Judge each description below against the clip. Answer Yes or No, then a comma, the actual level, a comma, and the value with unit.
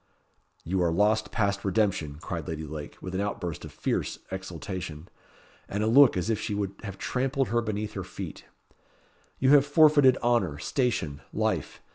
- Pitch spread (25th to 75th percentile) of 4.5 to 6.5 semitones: Yes, average, 5.0 semitones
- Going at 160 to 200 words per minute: Yes, average, 165 wpm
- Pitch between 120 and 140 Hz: No, low, 100 Hz